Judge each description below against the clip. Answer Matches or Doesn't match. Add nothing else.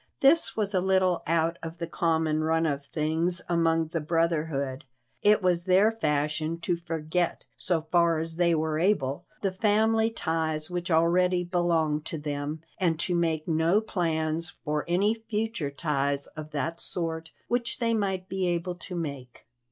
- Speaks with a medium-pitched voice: Matches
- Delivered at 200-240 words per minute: Doesn't match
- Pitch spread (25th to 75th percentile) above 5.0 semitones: Doesn't match